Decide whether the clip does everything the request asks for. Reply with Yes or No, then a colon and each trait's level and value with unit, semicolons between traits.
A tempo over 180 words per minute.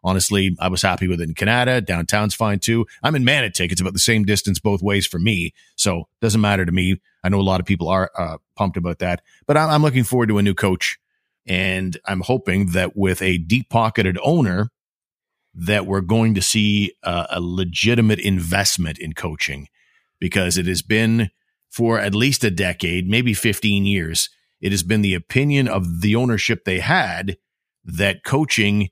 Yes: average, 190 wpm